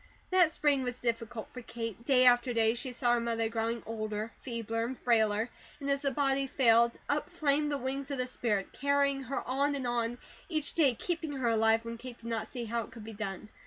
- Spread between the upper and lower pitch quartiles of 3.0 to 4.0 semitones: Yes, average, 3.3 semitones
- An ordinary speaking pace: No, fast, 220 wpm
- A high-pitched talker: Yes, high, 240 Hz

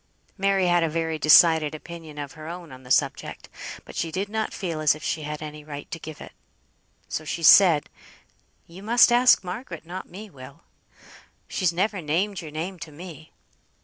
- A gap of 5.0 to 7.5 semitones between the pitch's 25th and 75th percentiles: No, average, 3.3 semitones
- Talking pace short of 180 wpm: No, average, 185 wpm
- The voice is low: No, medium, 165 Hz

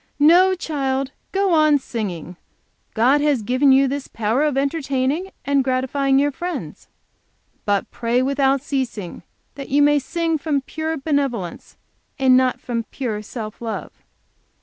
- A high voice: Yes, very high, 270 Hz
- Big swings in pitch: No, average, 2.9 semitones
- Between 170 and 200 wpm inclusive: No, average, 140 wpm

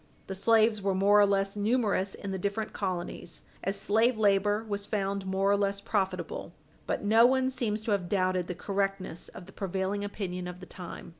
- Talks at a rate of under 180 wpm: No, average, 195 wpm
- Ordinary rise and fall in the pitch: No, narrow, 1.7 semitones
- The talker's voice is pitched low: No, high, 200 Hz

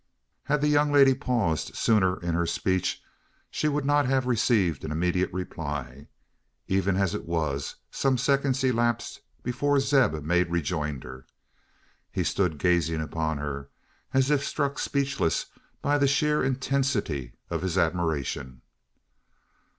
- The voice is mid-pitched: No, very low, 95 Hz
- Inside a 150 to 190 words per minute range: No, slow, 135 wpm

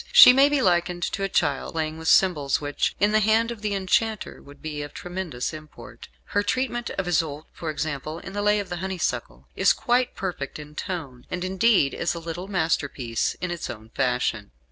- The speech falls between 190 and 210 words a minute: Yes, average, 200 wpm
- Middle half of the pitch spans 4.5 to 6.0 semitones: Yes, wide, 5.5 semitones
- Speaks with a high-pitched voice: No, medium, 175 Hz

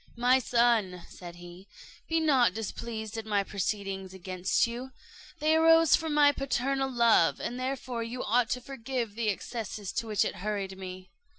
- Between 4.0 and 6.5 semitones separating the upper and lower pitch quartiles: Yes, average, 4.8 semitones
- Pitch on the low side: No, high, 230 Hz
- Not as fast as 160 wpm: No, average, 165 wpm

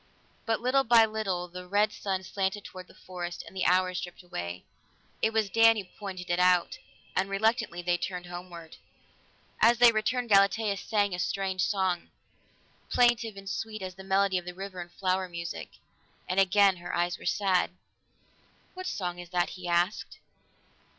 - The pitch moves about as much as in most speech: Yes, average, 3.0 semitones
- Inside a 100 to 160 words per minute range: No, average, 170 wpm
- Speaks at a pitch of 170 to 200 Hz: Yes, high, 190 Hz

